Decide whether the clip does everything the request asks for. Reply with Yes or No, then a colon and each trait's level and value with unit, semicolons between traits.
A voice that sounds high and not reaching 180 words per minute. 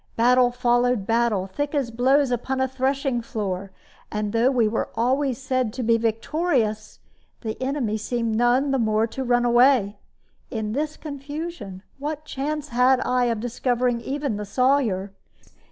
Yes: high, 245 Hz; average, 155 wpm